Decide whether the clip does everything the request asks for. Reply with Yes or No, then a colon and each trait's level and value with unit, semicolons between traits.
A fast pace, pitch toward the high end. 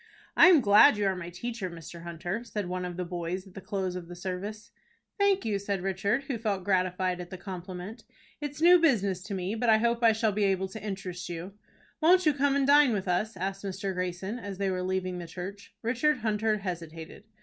Yes: fast, 220 wpm; high, 195 Hz